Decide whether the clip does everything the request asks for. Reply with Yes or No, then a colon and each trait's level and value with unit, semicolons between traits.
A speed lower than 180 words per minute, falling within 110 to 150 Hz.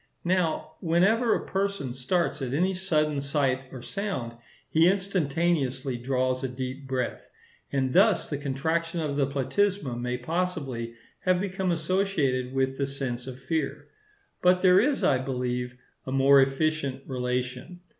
Yes: average, 145 wpm; medium, 140 Hz